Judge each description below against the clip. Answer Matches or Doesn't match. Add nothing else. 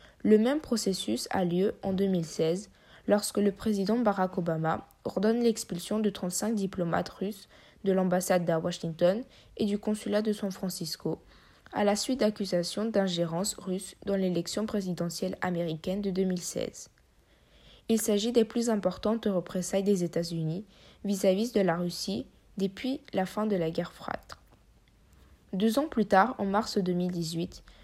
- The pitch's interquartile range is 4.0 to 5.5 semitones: Doesn't match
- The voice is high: Matches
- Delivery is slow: Matches